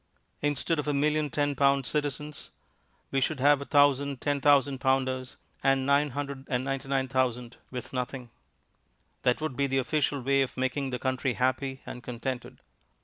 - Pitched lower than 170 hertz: Yes, low, 135 Hz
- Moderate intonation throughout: No, narrow, 1.7 semitones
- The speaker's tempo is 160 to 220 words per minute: No, average, 145 wpm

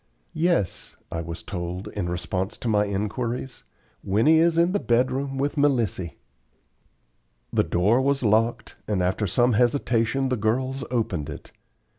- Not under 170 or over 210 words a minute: No, average, 145 wpm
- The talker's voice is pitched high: No, low, 115 Hz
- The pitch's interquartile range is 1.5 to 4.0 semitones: No, wide, 5.5 semitones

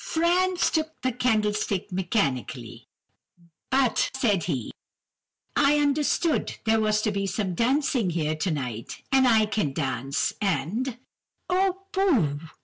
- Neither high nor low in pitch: No, high, 215 Hz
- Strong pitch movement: Yes, wide, 8.6 semitones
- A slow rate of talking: Yes, slow, 115 wpm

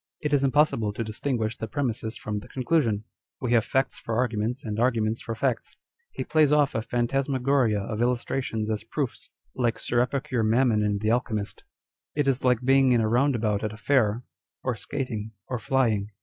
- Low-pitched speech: Yes, low, 120 Hz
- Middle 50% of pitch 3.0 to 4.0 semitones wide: Yes, average, 3.5 semitones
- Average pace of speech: Yes, average, 180 wpm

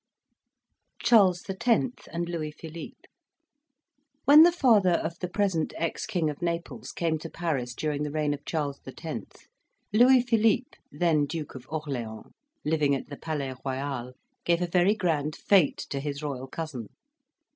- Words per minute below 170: Yes, average, 150 wpm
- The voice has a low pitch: No, medium, 160 Hz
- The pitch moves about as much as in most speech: Yes, average, 4.2 semitones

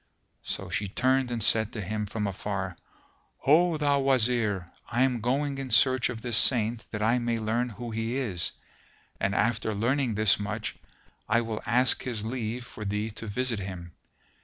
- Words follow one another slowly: No, average, 175 wpm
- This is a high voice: No, low, 115 Hz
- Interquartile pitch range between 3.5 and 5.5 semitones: No, average, 2.9 semitones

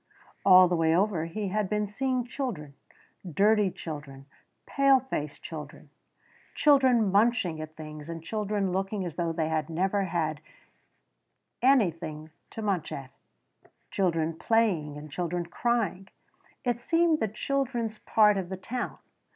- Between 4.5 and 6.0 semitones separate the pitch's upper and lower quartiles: Yes, wide, 5.6 semitones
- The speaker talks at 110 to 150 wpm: Yes, slow, 135 wpm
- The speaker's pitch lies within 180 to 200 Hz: Yes, high, 190 Hz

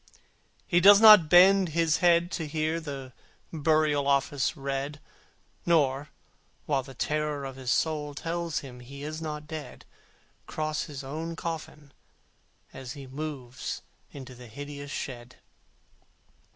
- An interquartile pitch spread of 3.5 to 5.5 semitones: No, average, 2.9 semitones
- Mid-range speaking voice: Yes, medium, 150 Hz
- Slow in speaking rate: Yes, slow, 130 wpm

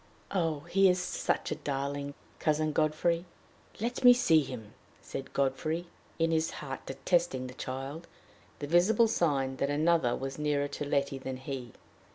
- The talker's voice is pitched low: No, medium, 150 Hz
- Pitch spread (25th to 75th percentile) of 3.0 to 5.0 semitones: Yes, average, 4.0 semitones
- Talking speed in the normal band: Yes, average, 155 wpm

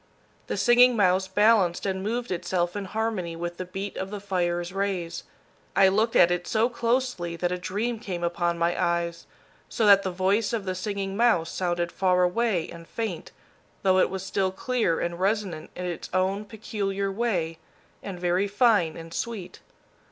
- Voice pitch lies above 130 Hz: Yes, high, 190 Hz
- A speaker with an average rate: Yes, average, 175 wpm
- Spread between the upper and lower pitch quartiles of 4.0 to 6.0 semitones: No, average, 3.2 semitones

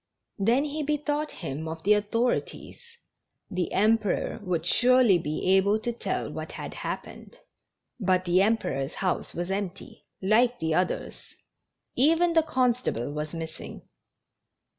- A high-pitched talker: Yes, high, 205 Hz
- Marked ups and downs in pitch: Yes, wide, 6.3 semitones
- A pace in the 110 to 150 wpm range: Yes, average, 140 wpm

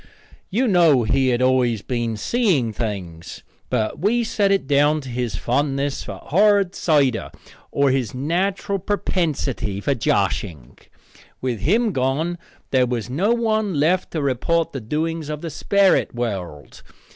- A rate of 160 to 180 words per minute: No, average, 145 wpm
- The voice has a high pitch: No, medium, 140 Hz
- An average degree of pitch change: No, wide, 7.0 semitones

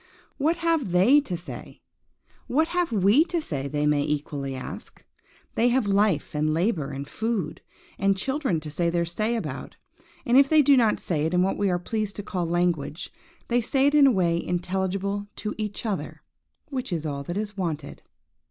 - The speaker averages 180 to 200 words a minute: Yes, average, 190 wpm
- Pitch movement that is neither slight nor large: No, wide, 6.4 semitones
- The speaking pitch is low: No, high, 195 Hz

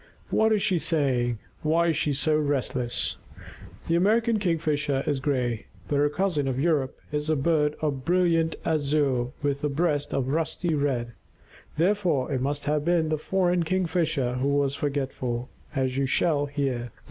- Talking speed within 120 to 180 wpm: Yes, average, 165 wpm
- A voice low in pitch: No, medium, 145 Hz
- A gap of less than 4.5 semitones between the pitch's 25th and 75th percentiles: Yes, average, 3.4 semitones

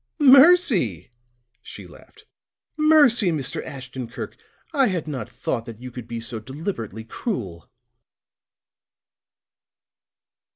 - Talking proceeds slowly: Yes, slow, 100 wpm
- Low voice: Yes, low, 130 Hz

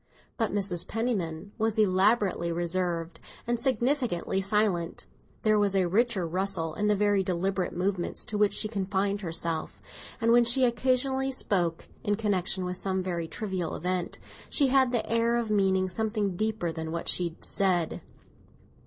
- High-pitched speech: Yes, high, 195 Hz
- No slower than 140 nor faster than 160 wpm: Yes, average, 155 wpm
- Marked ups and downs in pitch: No, average, 3.8 semitones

